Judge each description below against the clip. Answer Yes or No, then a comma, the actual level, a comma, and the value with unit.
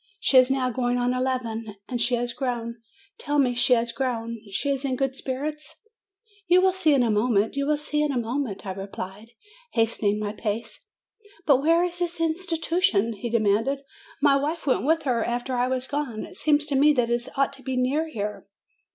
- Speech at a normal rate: No, fast, 210 wpm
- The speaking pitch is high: Yes, very high, 255 Hz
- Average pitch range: Yes, average, 3.9 semitones